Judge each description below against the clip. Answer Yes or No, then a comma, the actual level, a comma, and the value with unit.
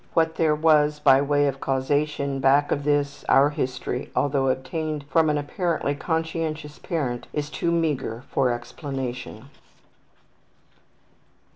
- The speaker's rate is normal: No, slow, 125 wpm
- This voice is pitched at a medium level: Yes, medium, 145 Hz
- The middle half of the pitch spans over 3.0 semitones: No, narrow, 2.4 semitones